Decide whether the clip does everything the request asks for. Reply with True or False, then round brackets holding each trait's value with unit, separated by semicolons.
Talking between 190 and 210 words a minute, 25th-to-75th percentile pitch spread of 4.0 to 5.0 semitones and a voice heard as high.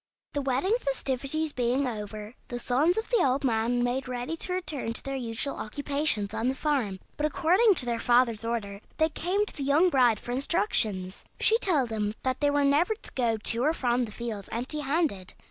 True (200 wpm; 4.7 semitones; 260 Hz)